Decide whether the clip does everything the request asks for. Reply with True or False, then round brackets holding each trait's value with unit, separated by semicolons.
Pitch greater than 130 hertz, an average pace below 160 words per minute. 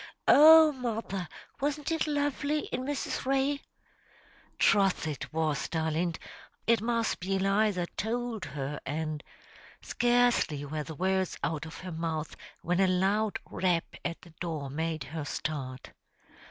True (185 Hz; 140 wpm)